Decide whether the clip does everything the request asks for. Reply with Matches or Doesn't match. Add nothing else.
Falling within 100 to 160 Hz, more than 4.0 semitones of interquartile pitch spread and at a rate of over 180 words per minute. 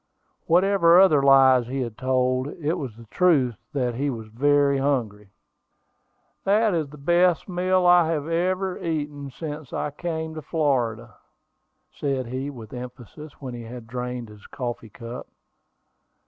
Doesn't match